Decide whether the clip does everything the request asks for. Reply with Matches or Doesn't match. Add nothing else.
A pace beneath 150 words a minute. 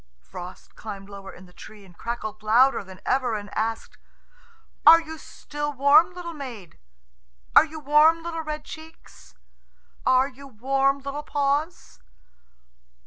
Matches